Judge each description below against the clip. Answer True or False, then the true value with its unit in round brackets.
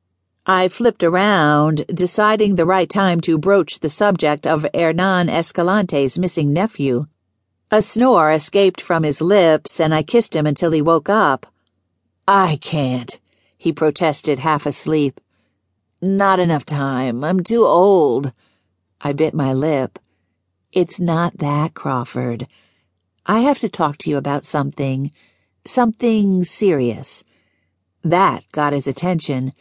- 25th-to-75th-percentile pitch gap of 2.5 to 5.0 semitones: False (5.6 semitones)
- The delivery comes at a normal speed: False (130 wpm)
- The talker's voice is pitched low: False (155 Hz)